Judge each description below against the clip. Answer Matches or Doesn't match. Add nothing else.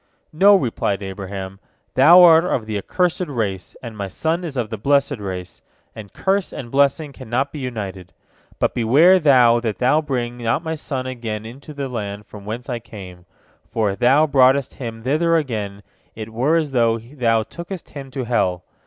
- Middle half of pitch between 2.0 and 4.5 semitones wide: Doesn't match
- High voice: Doesn't match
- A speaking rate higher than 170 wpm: Matches